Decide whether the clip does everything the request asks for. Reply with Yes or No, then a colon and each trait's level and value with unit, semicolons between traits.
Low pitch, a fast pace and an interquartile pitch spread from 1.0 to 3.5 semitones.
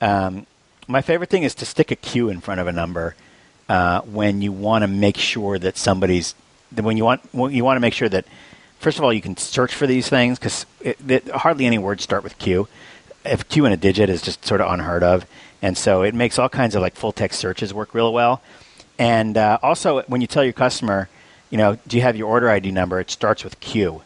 No: low, 110 Hz; fast, 235 wpm; average, 4.2 semitones